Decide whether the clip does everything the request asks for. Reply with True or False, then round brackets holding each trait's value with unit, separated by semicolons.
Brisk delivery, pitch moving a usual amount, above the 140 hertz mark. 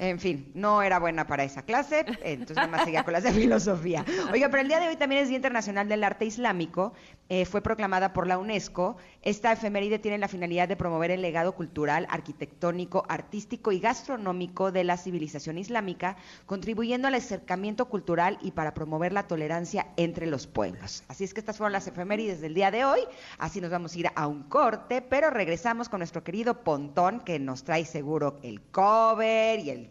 True (200 wpm; 4.5 semitones; 185 Hz)